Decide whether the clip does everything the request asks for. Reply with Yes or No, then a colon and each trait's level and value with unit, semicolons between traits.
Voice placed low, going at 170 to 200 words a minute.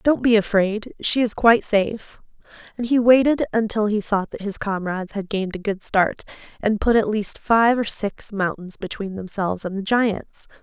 No: high, 210 Hz; average, 190 wpm